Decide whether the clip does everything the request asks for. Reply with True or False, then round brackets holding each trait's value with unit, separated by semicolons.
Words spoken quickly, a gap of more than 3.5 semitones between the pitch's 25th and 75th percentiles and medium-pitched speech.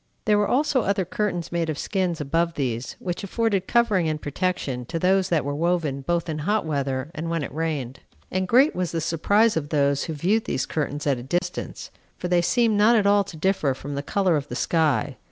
True (220 wpm; 4.9 semitones; 170 Hz)